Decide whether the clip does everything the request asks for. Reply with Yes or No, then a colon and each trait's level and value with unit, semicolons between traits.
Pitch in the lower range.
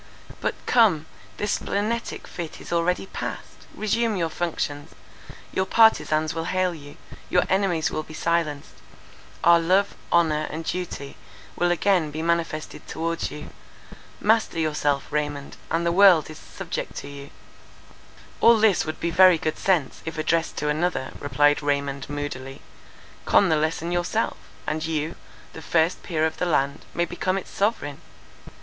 No: medium, 165 Hz